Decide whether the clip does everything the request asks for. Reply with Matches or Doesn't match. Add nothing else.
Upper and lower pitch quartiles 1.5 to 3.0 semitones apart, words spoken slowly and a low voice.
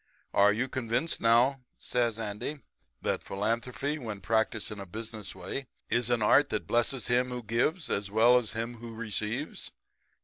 Doesn't match